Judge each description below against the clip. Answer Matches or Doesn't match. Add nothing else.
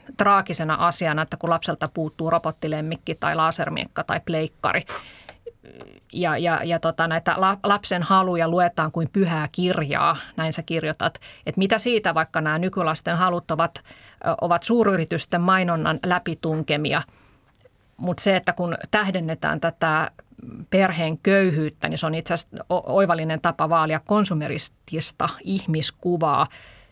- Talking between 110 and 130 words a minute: Matches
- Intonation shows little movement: Matches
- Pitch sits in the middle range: Matches